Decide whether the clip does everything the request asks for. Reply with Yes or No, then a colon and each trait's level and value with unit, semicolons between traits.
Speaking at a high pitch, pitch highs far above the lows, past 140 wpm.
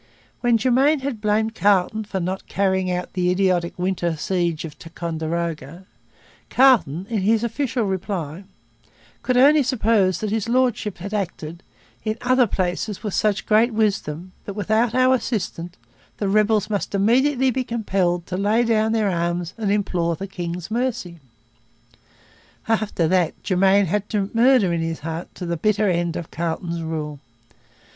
No: high, 195 Hz; average, 4.4 semitones; average, 150 wpm